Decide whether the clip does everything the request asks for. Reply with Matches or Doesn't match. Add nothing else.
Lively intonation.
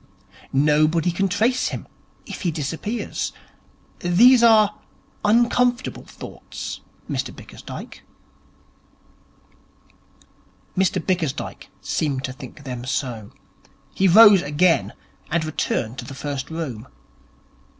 Matches